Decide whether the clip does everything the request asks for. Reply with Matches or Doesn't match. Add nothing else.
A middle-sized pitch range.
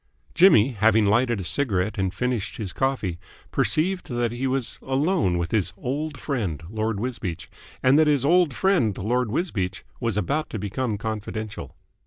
Matches